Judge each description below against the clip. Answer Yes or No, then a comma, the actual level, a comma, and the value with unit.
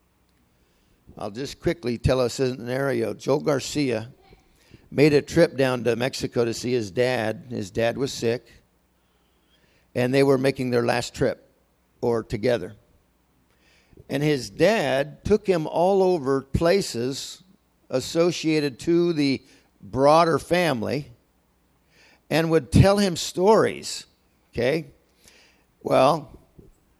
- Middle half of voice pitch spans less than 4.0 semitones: No, average, 4.5 semitones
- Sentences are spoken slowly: Yes, slow, 115 wpm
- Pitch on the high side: No, low, 130 Hz